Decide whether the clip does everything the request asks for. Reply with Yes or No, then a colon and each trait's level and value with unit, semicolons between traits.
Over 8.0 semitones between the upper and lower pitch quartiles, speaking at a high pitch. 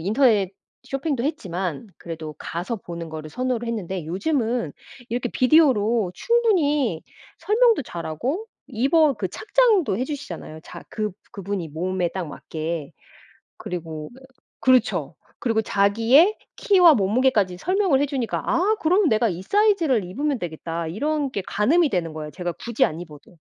Yes: wide, 8.8 semitones; high, 225 Hz